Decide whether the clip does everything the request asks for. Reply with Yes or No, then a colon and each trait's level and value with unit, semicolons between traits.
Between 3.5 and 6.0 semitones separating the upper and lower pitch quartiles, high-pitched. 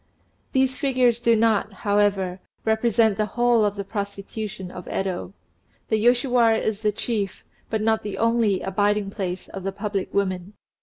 No: average, 2.7 semitones; high, 210 Hz